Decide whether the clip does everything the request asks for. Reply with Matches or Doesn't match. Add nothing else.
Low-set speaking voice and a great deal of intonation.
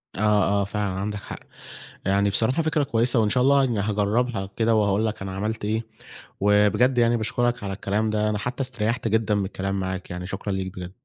Doesn't match